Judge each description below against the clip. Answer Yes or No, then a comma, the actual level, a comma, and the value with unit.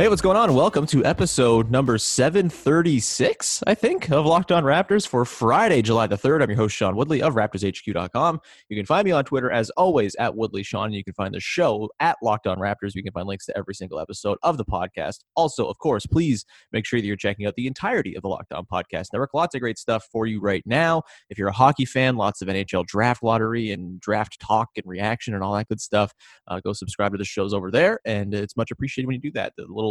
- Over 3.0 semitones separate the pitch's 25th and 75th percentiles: Yes, average, 4.7 semitones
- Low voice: Yes, low, 110 Hz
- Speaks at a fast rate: Yes, fast, 250 wpm